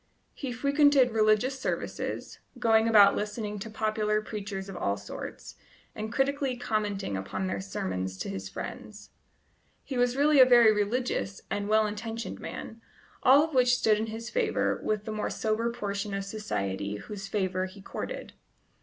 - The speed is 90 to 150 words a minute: No, average, 160 wpm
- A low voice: No, high, 215 Hz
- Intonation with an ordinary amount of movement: Yes, average, 3.7 semitones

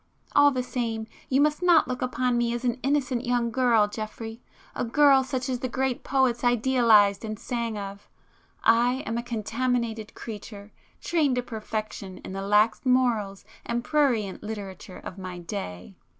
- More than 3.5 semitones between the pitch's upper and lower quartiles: No, average, 3.1 semitones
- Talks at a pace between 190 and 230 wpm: No, average, 155 wpm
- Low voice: No, high, 235 Hz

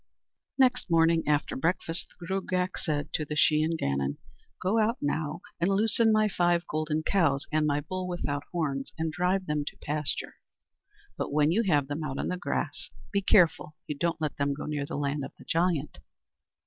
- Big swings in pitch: No, average, 3.7 semitones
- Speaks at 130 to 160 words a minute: No, average, 190 wpm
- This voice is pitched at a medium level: Yes, medium, 160 Hz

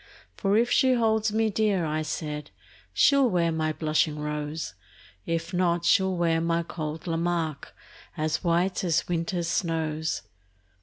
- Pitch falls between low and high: Yes, medium, 170 Hz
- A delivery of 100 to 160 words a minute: Yes, average, 140 wpm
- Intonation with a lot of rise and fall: No, average, 3.3 semitones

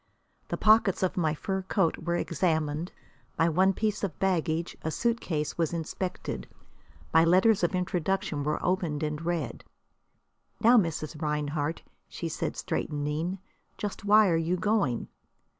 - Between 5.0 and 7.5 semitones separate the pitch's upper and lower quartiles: No, average, 3.7 semitones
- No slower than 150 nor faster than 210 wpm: No, average, 140 wpm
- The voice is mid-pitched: Yes, medium, 170 Hz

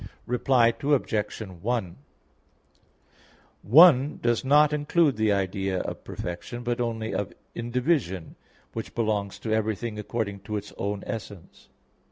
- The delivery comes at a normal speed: No, slow, 120 wpm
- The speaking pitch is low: Yes, low, 115 Hz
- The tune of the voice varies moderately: Yes, average, 3.4 semitones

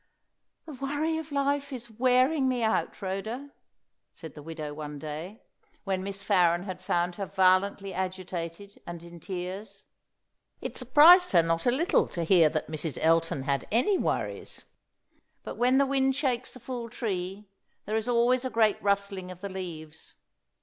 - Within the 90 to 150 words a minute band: No, average, 165 wpm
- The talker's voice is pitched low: No, high, 200 Hz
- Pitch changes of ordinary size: No, wide, 6.6 semitones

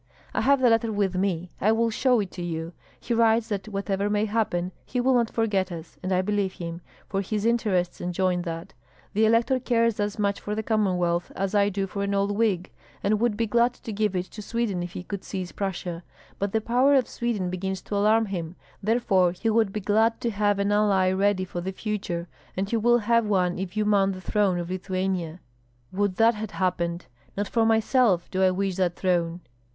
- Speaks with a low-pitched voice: No, high, 200 Hz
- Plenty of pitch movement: No, average, 3.2 semitones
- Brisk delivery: Yes, fast, 215 wpm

